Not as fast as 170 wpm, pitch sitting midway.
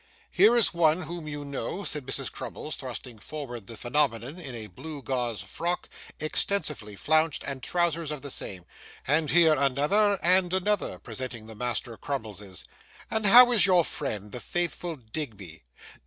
Yes: average, 155 wpm; medium, 145 Hz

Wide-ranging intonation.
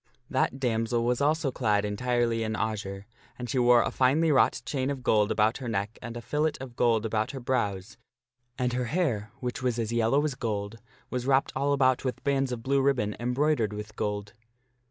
No: average, 3.4 semitones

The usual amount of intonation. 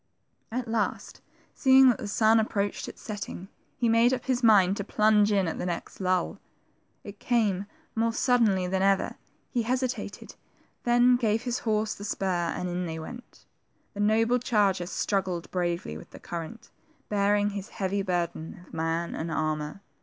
Yes: average, 4.0 semitones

